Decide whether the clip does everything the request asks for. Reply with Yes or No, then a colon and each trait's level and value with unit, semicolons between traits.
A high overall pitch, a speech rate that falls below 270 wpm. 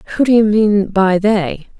Yes: high, 205 Hz; average, 200 wpm